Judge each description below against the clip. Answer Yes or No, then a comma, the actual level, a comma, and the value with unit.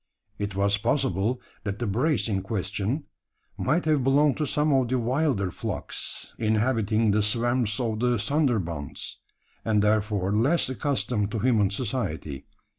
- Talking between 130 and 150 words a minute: Yes, average, 140 wpm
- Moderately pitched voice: No, low, 110 Hz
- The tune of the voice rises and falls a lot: No, average, 4.3 semitones